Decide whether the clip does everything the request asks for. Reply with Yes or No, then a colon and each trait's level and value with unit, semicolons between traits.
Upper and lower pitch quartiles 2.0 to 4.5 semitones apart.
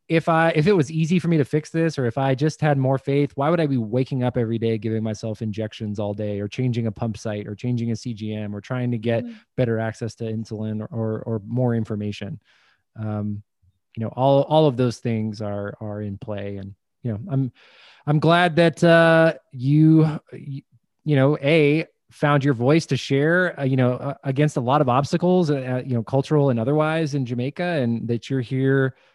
No: average, 5.0 semitones